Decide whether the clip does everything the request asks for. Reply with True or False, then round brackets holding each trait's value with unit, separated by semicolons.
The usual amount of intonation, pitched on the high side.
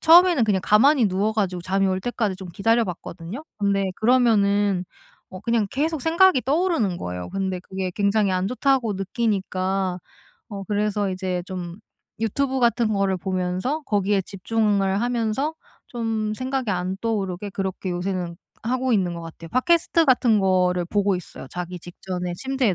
True (4.2 semitones; 200 Hz)